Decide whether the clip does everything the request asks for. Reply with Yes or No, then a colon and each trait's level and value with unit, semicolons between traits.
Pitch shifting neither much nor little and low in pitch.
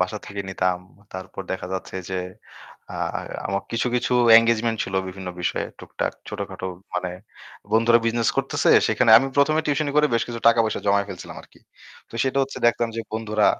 Yes: average, 3.6 semitones; low, 115 Hz